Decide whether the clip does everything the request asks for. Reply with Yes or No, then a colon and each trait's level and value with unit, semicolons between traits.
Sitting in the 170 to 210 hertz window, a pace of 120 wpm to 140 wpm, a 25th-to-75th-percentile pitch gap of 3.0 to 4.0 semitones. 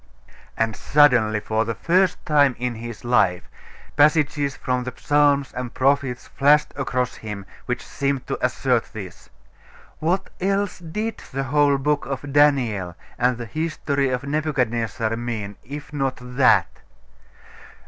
No: low, 135 Hz; slow, 135 wpm; average, 3.7 semitones